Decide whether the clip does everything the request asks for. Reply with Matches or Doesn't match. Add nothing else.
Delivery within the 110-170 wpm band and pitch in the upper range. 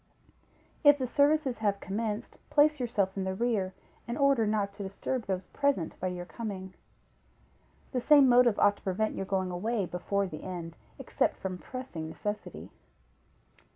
Matches